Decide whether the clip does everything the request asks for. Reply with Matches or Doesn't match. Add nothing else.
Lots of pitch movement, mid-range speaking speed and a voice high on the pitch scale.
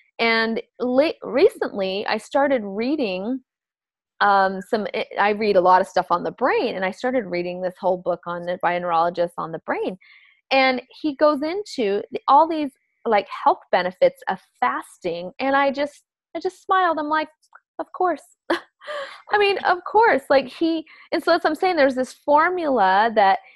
Matches